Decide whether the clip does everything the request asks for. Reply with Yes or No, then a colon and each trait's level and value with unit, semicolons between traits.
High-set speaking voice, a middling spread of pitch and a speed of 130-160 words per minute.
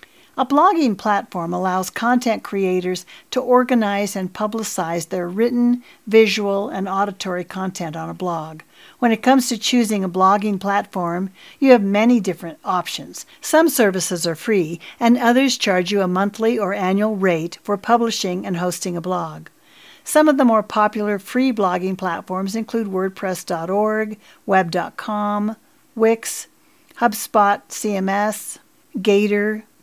Yes: high, 205 Hz; average, 4.0 semitones; slow, 135 wpm